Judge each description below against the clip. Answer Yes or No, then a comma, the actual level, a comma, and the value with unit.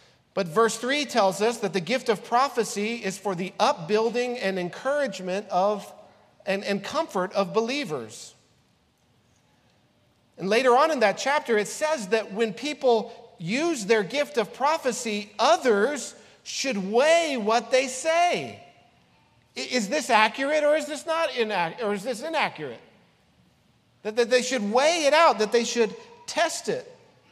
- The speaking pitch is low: No, high, 235 Hz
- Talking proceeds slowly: No, average, 150 wpm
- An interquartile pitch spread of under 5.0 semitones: No, wide, 5.5 semitones